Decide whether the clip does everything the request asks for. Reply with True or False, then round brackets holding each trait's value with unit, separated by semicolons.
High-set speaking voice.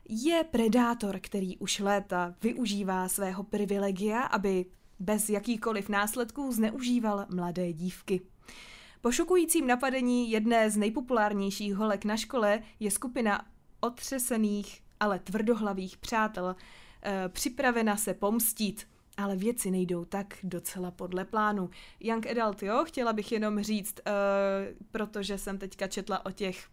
True (205 Hz)